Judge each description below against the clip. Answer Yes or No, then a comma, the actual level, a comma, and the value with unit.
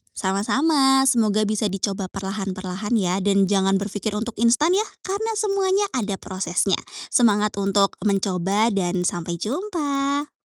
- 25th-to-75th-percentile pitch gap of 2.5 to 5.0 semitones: No, wide, 5.6 semitones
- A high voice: Yes, high, 210 Hz